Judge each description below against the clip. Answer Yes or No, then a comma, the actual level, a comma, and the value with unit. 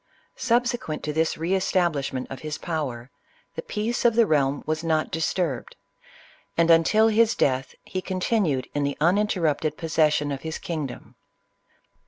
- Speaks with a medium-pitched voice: Yes, medium, 160 Hz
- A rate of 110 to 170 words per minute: Yes, average, 150 wpm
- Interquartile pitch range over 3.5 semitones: Yes, average, 4.3 semitones